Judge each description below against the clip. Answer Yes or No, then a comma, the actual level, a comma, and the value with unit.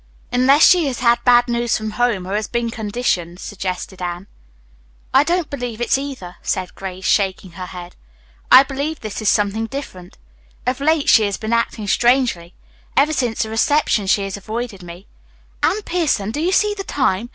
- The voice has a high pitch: Yes, high, 230 Hz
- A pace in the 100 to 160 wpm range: No, average, 180 wpm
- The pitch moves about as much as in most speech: No, wide, 5.7 semitones